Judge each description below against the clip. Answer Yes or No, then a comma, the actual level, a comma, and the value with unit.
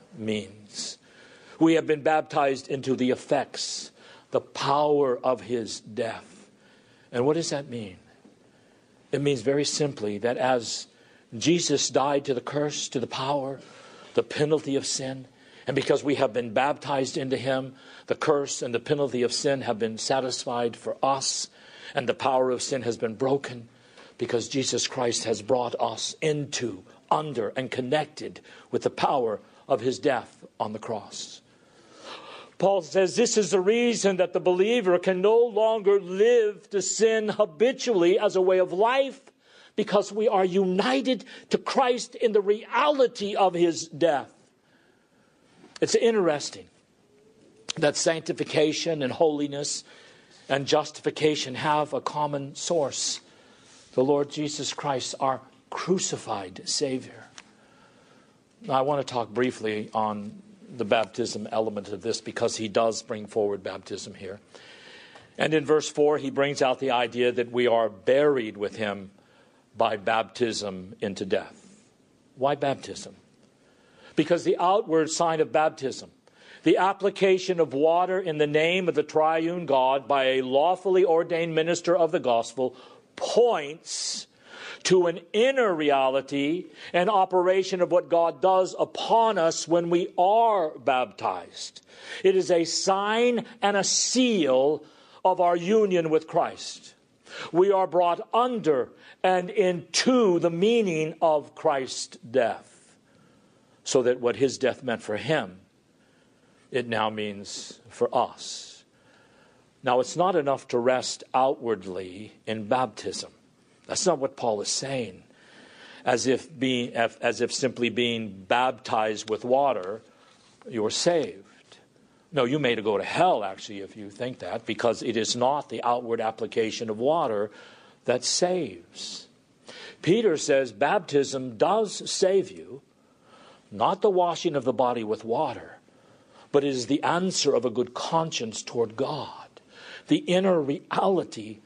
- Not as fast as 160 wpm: Yes, average, 140 wpm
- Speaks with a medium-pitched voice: Yes, medium, 150 Hz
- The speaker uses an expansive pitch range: Yes, wide, 6.4 semitones